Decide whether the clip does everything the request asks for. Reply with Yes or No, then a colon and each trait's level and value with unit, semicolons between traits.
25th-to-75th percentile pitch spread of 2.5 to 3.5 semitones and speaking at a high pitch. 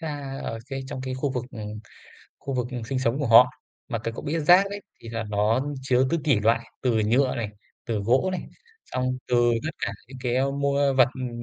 No: average, 3.0 semitones; low, 130 Hz